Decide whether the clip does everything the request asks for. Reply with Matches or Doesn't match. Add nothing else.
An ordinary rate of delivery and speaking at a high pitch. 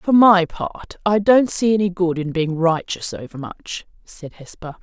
Doesn't match